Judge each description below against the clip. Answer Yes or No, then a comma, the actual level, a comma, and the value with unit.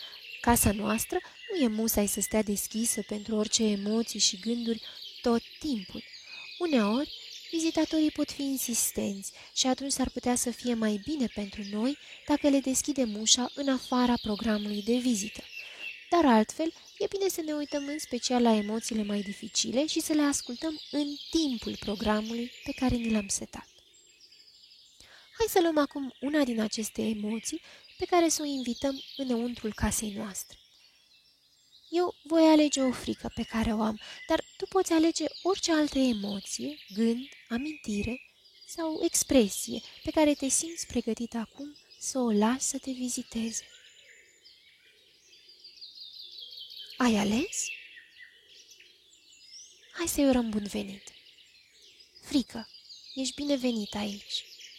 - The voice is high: Yes, very high, 260 Hz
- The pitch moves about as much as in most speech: No, wide, 6.2 semitones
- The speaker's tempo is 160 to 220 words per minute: No, average, 135 wpm